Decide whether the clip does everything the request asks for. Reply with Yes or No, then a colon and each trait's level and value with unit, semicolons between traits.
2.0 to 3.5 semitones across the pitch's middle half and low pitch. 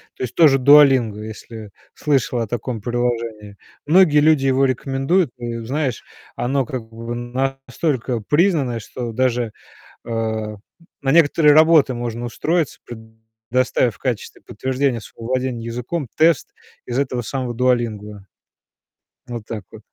Yes: average, 3.2 semitones; low, 125 Hz